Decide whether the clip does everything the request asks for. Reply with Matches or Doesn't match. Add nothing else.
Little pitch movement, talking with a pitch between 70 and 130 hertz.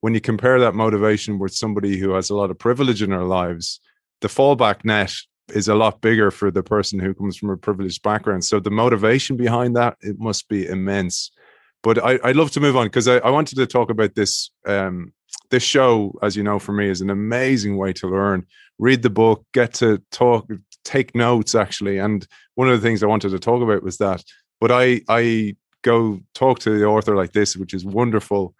Doesn't match